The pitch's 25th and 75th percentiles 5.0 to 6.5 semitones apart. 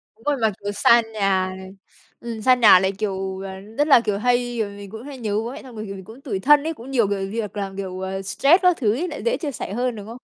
No: average, 4.3 semitones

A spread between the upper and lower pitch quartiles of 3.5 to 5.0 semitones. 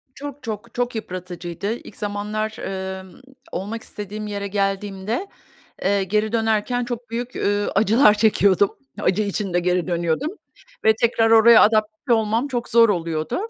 No: average, 2.9 semitones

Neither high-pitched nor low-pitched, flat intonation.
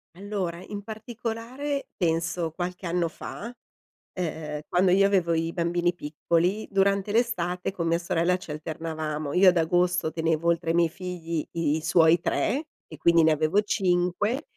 No: medium, 175 Hz; average, 3.0 semitones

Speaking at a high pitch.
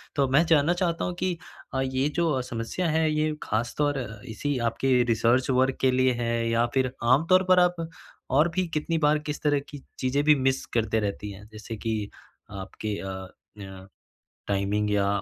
No: low, 130 Hz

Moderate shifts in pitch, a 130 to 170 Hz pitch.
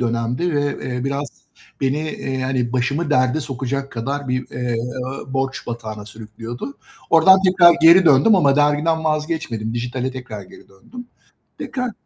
Yes: average, 4.3 semitones; low, 135 Hz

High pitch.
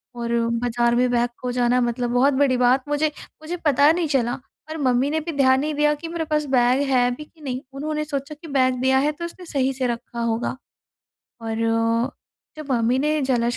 Yes: very high, 260 Hz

